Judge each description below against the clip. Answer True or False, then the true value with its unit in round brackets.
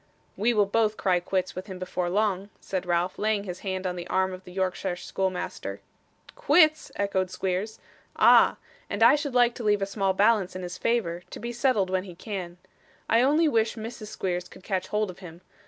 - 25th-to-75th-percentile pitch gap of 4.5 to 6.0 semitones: False (3.2 semitones)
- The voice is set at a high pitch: True (195 Hz)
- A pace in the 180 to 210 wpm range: True (205 wpm)